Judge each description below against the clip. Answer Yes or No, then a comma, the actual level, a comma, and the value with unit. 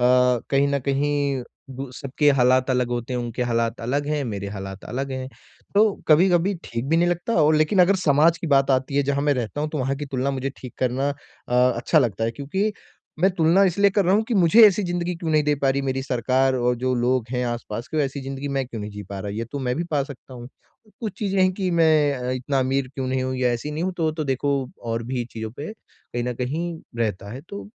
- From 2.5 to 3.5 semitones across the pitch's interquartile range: No, average, 4.2 semitones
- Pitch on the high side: No, low, 135 Hz